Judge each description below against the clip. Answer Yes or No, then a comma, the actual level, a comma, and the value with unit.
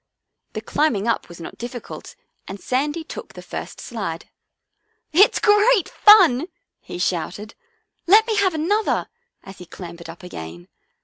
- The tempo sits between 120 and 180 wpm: Yes, average, 160 wpm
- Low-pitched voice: No, very high, 255 Hz